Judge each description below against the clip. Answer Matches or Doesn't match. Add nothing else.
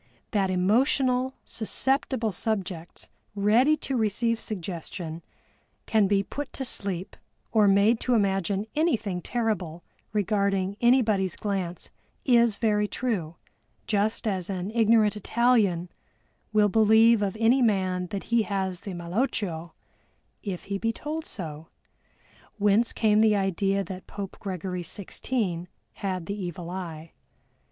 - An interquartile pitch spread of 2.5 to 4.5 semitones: Matches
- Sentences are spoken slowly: Matches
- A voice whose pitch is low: Doesn't match